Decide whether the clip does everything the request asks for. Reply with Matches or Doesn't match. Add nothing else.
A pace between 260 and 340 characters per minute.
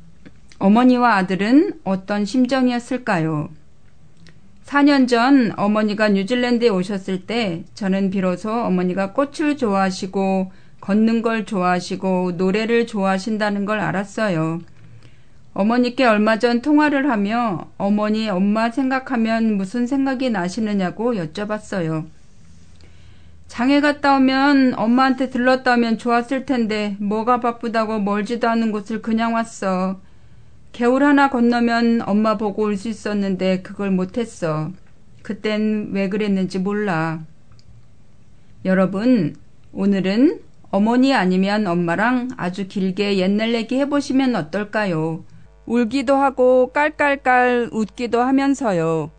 Matches